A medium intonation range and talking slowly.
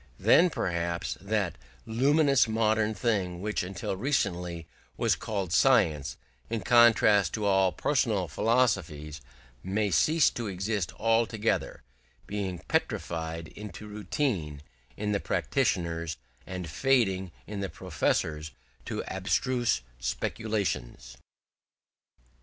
Yes: average, 4.7 semitones; slow, 100 wpm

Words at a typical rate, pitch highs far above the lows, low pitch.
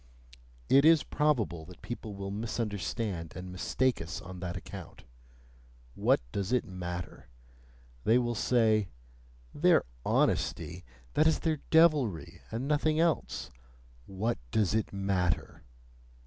No: slow, 120 wpm; wide, 5.7 semitones; low, 105 Hz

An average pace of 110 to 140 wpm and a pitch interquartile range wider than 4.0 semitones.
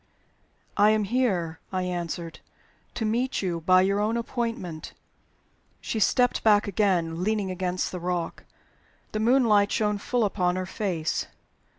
No: slow, 135 wpm; average, 3.4 semitones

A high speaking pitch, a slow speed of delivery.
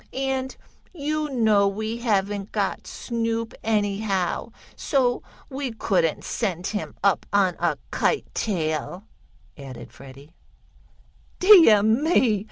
Yes: high, 215 Hz; slow, 105 wpm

